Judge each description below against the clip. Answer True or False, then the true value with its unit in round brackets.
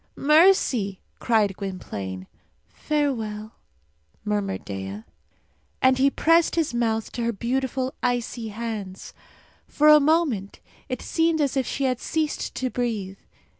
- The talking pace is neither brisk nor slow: False (125 wpm)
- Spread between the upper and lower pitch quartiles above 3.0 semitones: True (5.5 semitones)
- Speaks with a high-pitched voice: True (240 Hz)